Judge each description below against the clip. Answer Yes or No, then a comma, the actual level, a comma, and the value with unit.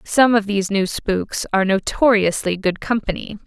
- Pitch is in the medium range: No, high, 205 Hz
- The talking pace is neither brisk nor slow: Yes, average, 155 wpm